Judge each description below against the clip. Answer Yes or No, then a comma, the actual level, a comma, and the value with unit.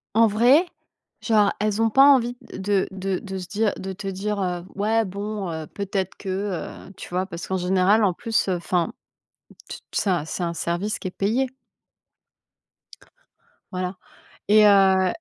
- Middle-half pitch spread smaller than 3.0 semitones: Yes, narrow, 2.5 semitones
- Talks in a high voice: Yes, high, 195 Hz